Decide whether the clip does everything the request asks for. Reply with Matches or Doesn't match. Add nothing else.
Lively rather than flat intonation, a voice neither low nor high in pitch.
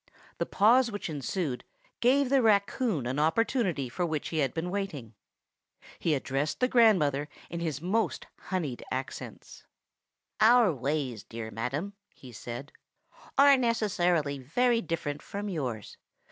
Matches